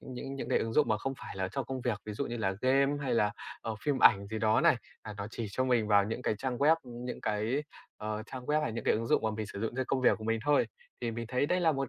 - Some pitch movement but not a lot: Yes, average, 3.6 semitones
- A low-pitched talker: Yes, low, 120 Hz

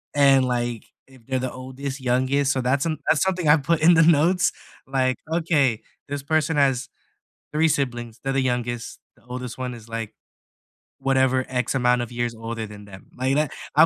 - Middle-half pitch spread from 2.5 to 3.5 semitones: Yes, average, 2.8 semitones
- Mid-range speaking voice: No, low, 130 Hz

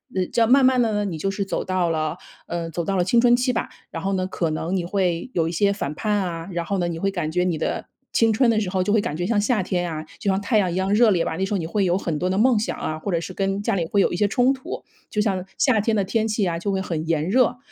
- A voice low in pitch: No, high, 195 Hz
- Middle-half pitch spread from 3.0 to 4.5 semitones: Yes, average, 3.6 semitones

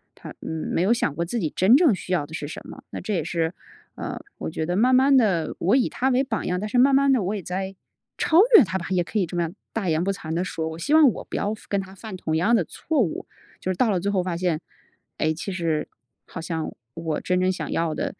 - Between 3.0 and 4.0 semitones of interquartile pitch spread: No, average, 5.0 semitones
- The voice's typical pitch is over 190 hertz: No, medium, 185 Hz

